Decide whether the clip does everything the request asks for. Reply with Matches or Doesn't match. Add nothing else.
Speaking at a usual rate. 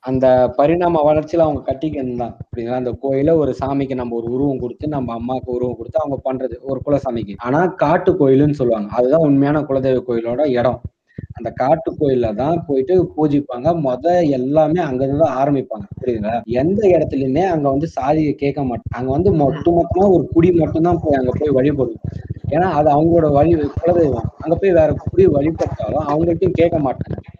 Doesn't match